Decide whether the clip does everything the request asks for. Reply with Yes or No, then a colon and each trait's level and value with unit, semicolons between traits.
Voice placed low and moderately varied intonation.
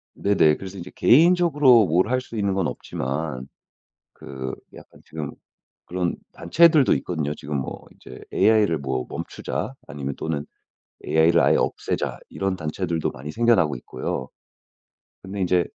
No: very low, 85 Hz; wide, 5.9 semitones